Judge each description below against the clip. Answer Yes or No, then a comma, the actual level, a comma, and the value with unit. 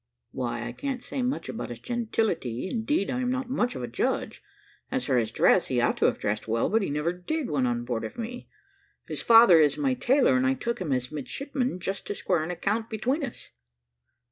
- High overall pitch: Yes, high, 205 Hz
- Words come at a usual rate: No, fast, 220 wpm